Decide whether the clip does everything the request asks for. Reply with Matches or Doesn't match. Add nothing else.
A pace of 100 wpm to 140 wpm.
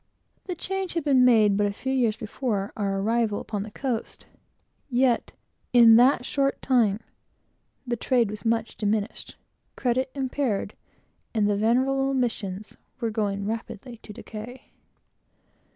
Matches